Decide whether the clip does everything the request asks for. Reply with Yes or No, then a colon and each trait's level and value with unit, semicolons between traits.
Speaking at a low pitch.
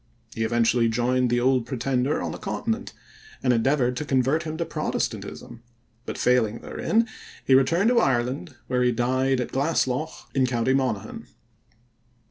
Yes: low, 130 Hz